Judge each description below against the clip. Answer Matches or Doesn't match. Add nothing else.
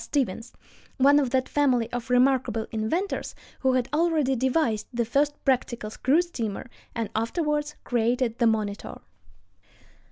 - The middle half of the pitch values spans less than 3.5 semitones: Doesn't match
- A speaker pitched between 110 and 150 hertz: Doesn't match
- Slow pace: Matches